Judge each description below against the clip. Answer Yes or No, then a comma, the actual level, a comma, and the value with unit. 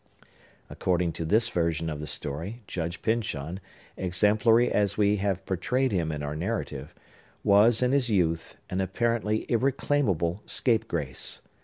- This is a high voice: No, very low, 95 Hz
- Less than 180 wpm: Yes, slow, 135 wpm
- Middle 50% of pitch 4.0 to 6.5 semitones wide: Yes, wide, 5.4 semitones